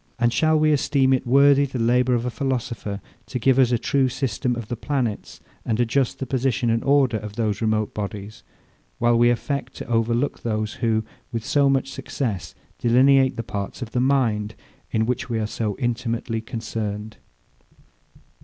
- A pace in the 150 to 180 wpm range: Yes, average, 175 wpm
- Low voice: Yes, low, 120 Hz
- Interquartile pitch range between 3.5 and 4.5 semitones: No, average, 3.1 semitones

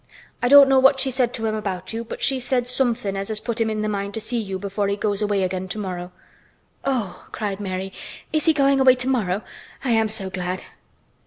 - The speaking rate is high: Yes, fast, 220 wpm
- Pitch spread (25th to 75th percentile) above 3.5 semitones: Yes, average, 4.3 semitones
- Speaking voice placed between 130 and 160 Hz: No, high, 215 Hz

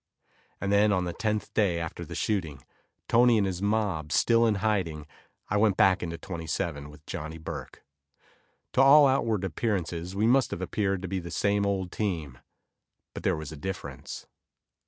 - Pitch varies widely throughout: No, average, 4.3 semitones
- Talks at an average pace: Yes, average, 175 wpm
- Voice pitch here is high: No, very low, 95 Hz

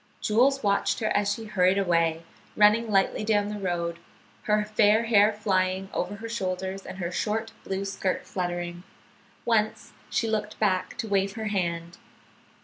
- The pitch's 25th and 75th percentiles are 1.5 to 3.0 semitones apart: Yes, narrow, 2.5 semitones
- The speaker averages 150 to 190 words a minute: Yes, average, 155 wpm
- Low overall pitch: No, high, 200 Hz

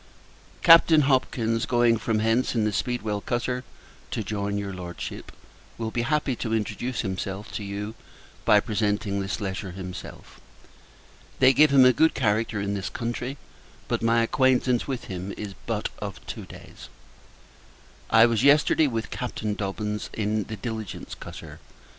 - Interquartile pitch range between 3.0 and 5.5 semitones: Yes, average, 3.4 semitones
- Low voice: Yes, low, 110 Hz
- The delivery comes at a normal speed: Yes, average, 150 wpm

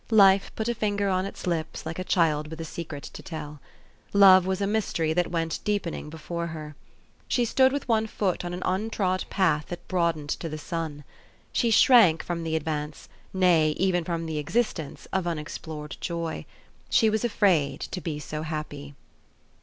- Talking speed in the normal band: Yes, average, 180 wpm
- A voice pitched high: No, medium, 170 Hz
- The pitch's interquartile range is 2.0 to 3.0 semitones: No, average, 3.9 semitones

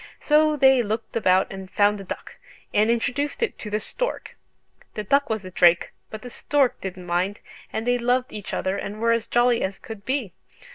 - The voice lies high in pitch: Yes, high, 220 Hz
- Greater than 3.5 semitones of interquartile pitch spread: Yes, average, 4.2 semitones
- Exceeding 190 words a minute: Yes, average, 200 wpm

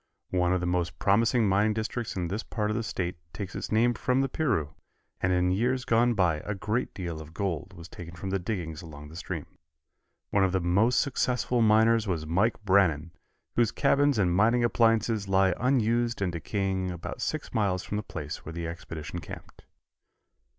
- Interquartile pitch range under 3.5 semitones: No, average, 4.5 semitones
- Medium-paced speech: Yes, average, 190 wpm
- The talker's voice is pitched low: Yes, low, 100 Hz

